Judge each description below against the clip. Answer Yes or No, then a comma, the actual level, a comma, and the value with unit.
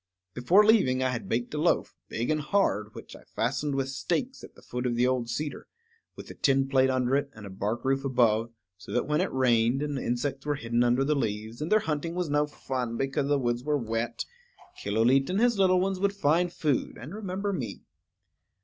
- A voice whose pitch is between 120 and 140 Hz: Yes, low, 135 Hz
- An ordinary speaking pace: No, fast, 215 wpm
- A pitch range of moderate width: Yes, average, 4.2 semitones